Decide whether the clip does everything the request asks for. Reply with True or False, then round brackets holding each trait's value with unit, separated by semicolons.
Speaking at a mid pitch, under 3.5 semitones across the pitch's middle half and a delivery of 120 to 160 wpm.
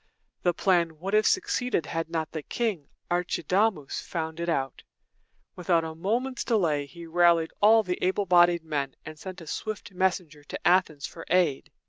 False (175 Hz; 3.0 semitones; 175 wpm)